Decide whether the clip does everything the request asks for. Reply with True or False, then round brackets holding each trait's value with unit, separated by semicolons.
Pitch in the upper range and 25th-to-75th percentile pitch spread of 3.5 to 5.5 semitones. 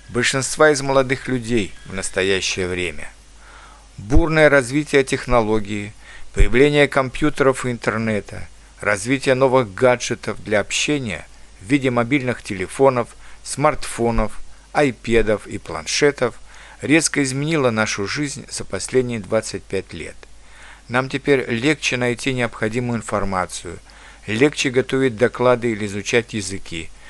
False (120 Hz; 4.7 semitones)